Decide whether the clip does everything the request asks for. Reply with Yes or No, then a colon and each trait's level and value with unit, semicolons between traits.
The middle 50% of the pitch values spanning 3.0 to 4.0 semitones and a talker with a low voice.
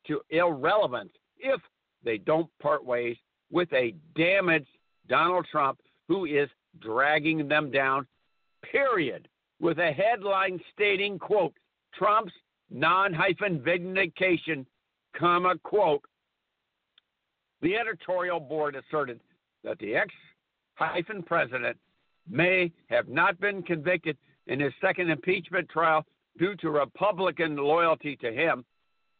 No: average, 3.5 semitones; medium, 170 Hz